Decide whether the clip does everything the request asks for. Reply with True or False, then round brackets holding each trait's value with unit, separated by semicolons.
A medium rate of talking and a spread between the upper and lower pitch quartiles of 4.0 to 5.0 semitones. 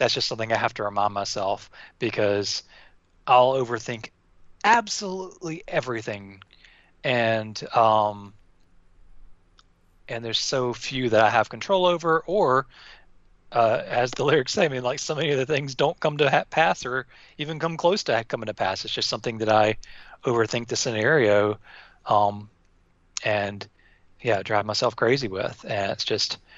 True (155 wpm; 4.5 semitones)